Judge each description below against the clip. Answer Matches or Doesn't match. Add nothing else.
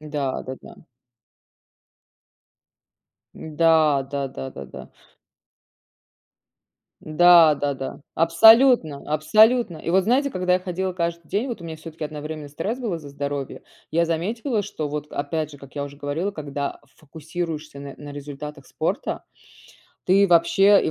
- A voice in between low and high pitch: Matches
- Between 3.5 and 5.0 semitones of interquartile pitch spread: Matches